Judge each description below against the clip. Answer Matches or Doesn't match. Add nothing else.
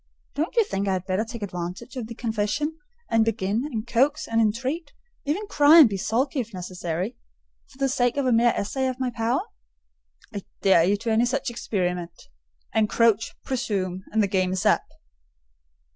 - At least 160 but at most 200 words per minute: Matches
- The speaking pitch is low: Doesn't match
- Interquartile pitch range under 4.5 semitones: Doesn't match